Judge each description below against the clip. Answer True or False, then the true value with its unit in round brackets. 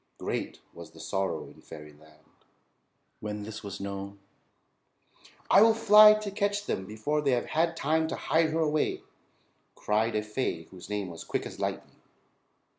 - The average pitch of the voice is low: True (110 Hz)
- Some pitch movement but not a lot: False (8.7 semitones)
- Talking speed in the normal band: True (160 wpm)